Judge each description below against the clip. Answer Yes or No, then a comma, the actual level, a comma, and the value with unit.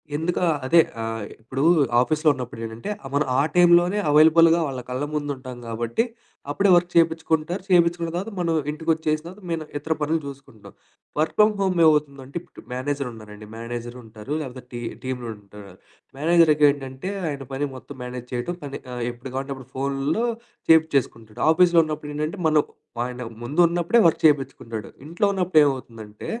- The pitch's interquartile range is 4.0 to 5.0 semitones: Yes, average, 4.7 semitones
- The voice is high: No, medium, 145 Hz